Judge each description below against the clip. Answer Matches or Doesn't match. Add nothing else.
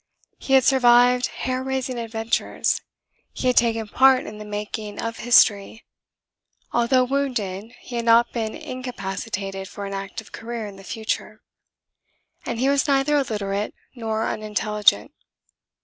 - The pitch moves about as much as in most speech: Matches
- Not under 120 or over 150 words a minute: Matches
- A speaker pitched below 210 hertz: Doesn't match